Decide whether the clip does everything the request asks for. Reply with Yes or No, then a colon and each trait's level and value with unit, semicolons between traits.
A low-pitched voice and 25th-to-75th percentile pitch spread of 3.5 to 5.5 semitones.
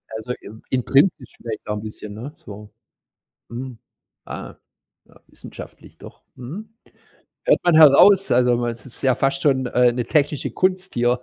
Yes: low, 125 Hz; average, 4.0 semitones